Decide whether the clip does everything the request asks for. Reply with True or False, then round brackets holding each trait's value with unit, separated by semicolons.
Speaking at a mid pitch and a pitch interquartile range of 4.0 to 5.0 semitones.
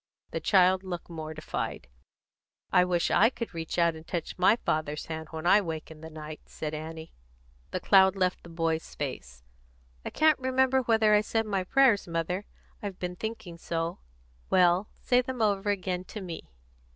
True (180 Hz; 4.3 semitones)